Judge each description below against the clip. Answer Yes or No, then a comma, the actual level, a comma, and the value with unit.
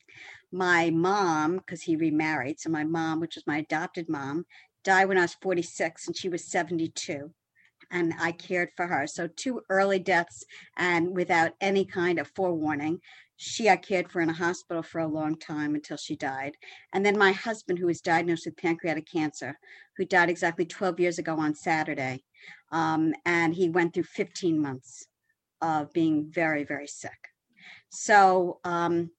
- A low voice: No, medium, 170 Hz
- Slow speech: No, average, 170 wpm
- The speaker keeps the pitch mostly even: Yes, narrow, 2.3 semitones